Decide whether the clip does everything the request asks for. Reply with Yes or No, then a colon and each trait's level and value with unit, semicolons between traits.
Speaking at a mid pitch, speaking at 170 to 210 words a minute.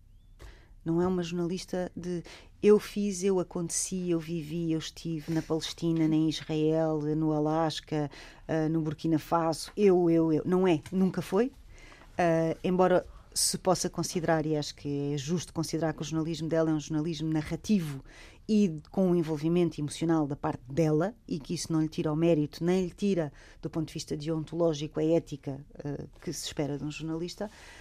Yes: medium, 160 Hz; average, 180 wpm